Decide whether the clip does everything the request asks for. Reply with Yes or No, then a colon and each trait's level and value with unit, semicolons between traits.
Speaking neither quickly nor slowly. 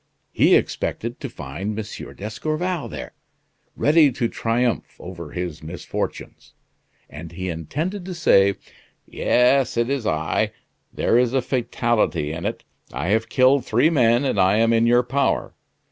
Yes: average, 145 wpm